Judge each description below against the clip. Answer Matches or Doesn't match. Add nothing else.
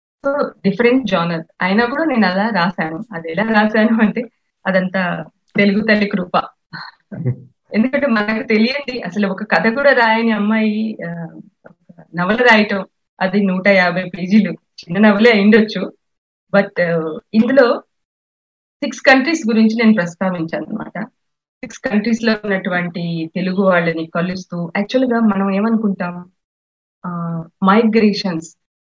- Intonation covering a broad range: Doesn't match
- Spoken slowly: Doesn't match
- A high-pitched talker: Matches